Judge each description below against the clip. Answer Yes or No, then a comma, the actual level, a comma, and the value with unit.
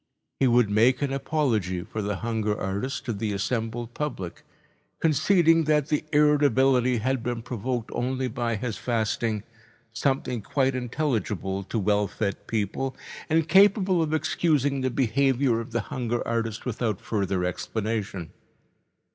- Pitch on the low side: Yes, low, 120 Hz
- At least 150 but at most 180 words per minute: No, average, 140 wpm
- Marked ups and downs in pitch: No, average, 4.1 semitones